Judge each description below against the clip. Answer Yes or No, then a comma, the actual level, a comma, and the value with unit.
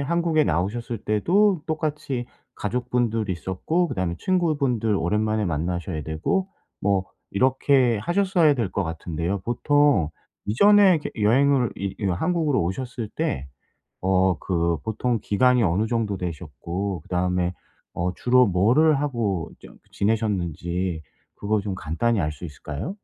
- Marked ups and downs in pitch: Yes, wide, 6.7 semitones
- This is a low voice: Yes, low, 105 Hz